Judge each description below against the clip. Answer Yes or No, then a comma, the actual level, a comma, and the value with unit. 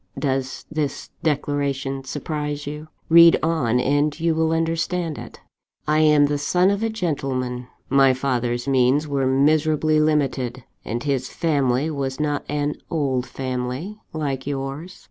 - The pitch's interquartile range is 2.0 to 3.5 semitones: Yes, average, 2.9 semitones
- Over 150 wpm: No, average, 140 wpm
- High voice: No, medium, 145 Hz